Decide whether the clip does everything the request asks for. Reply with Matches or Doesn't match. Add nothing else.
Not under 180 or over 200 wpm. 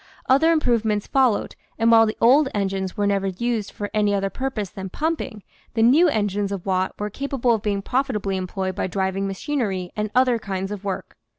Matches